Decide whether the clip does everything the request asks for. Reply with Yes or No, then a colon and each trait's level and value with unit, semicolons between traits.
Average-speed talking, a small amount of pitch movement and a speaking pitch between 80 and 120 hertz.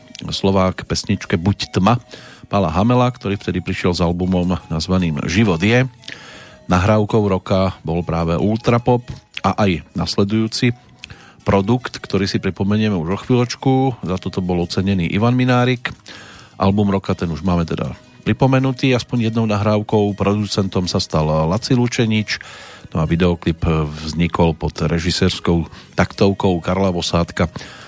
No: average, 125 wpm; average, 4.1 semitones; low, 100 Hz